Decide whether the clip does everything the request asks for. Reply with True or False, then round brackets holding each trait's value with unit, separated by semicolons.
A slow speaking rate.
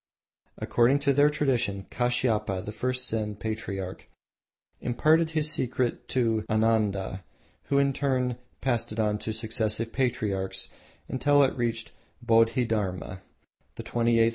True (130 wpm)